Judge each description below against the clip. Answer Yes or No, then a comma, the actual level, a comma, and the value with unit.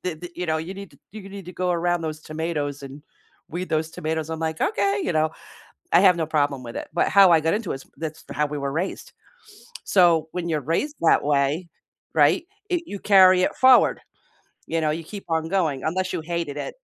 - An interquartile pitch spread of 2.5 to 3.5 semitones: Yes, average, 3.0 semitones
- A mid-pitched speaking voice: Yes, medium, 165 Hz